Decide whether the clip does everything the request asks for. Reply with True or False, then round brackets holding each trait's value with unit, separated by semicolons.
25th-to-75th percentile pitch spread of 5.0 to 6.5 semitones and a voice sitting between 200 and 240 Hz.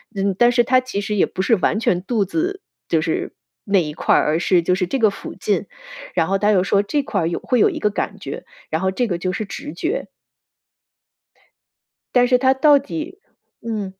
True (5.4 semitones; 205 Hz)